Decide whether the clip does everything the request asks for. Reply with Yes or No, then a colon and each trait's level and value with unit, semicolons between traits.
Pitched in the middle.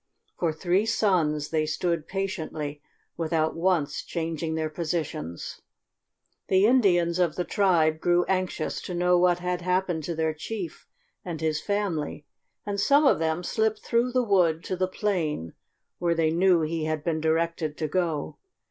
Yes: medium, 170 Hz